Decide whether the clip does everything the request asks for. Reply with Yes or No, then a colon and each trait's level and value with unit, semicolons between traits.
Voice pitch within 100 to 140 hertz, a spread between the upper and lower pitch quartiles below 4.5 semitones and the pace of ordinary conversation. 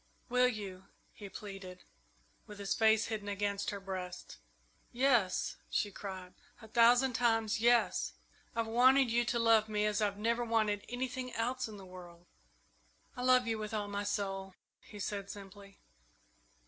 No: high, 215 Hz; average, 2.9 semitones; average, 155 wpm